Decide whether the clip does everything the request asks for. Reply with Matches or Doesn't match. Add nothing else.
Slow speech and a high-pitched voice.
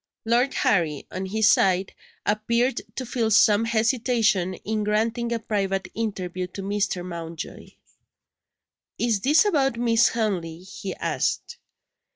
Matches